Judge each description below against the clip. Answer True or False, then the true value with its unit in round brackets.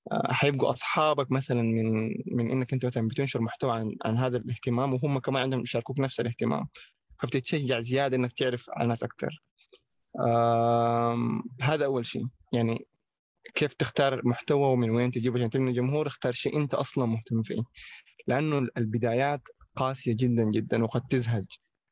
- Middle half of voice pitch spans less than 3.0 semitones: True (2.5 semitones)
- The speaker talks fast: True (145 wpm)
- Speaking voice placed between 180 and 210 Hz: False (125 Hz)